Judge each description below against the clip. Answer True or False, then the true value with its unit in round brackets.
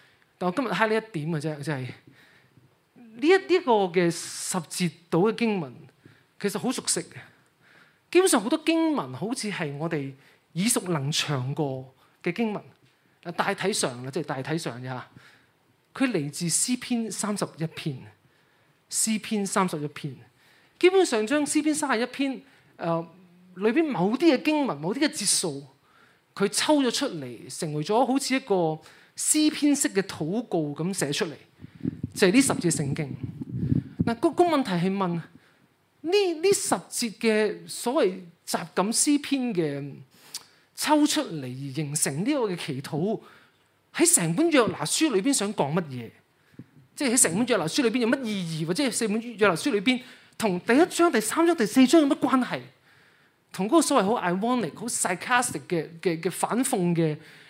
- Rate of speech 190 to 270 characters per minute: True (245 characters per minute)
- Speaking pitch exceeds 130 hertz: True (190 Hz)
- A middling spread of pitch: False (8.1 semitones)